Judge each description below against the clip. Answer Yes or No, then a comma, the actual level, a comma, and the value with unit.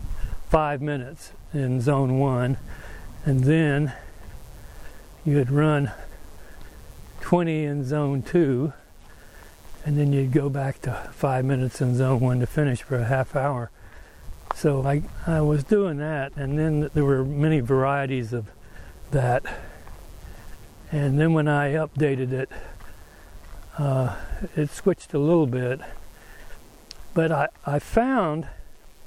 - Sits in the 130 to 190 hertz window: Yes, medium, 140 Hz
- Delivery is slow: Yes, slow, 125 wpm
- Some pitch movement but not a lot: Yes, average, 4.0 semitones